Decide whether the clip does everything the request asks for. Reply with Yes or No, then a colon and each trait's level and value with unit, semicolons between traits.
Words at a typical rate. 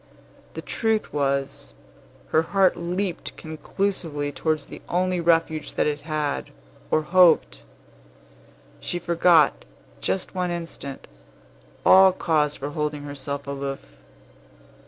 No: slow, 110 wpm